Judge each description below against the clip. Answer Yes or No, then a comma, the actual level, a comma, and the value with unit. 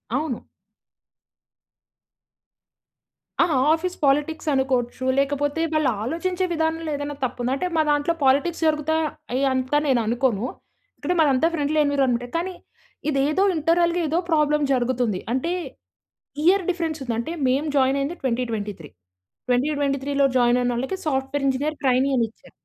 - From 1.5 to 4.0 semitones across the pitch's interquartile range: Yes, average, 3.7 semitones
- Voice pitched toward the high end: Yes, very high, 280 Hz